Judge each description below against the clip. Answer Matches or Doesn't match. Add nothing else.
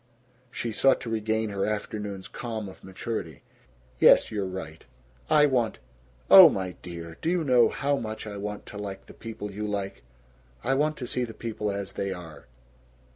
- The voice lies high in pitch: Doesn't match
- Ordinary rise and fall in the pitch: Matches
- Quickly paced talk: Doesn't match